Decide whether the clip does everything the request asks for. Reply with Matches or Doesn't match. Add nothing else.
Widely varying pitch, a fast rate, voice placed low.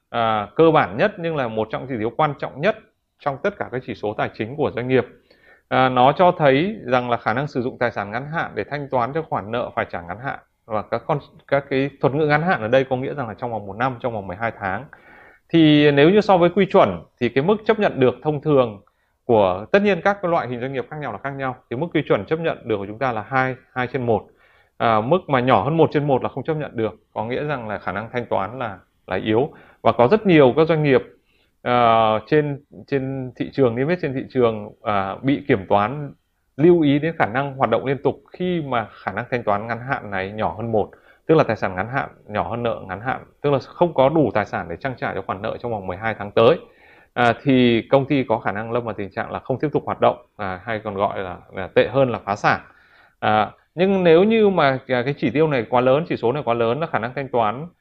Doesn't match